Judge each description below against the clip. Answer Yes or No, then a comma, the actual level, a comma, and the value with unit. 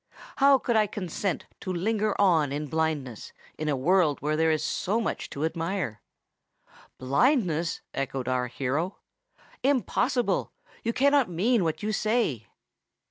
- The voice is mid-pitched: Yes, medium, 170 Hz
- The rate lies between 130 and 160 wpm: Yes, slow, 135 wpm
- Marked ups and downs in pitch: Yes, wide, 6.8 semitones